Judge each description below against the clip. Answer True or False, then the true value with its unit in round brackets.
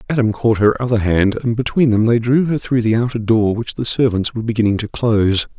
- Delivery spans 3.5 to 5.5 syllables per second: False (5.9 syllables/s)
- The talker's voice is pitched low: True (115 Hz)